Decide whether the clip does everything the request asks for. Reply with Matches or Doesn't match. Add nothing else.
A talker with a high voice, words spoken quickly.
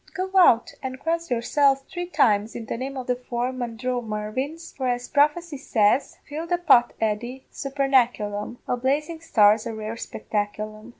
Doesn't match